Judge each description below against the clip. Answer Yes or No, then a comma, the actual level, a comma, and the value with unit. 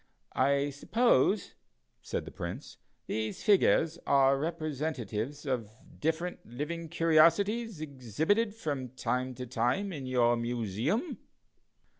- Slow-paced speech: Yes, slow, 105 wpm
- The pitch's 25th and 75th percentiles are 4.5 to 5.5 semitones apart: Yes, average, 5.0 semitones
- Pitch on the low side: No, medium, 145 Hz